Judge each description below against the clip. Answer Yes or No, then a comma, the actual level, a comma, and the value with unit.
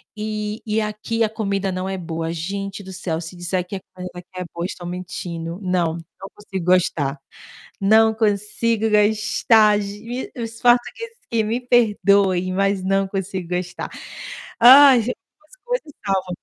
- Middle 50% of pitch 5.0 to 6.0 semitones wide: No, average, 3.3 semitones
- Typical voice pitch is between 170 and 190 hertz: No, high, 200 Hz